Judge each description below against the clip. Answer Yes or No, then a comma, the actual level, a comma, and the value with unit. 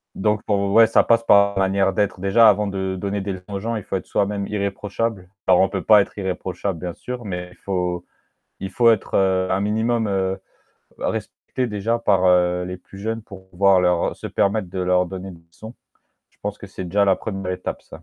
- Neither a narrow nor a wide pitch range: No, narrow, 2.1 semitones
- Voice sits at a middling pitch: No, very low, 95 Hz